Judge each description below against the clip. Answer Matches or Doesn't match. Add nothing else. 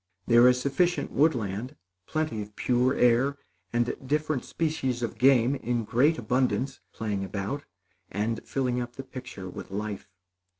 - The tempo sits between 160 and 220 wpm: Doesn't match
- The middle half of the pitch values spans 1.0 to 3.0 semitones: Doesn't match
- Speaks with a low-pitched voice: Matches